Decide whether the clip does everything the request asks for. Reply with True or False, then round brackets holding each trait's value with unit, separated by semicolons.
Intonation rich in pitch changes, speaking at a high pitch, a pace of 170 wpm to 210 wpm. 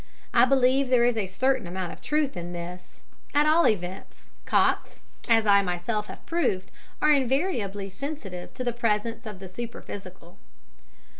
False (5.7 semitones; 220 Hz; 155 wpm)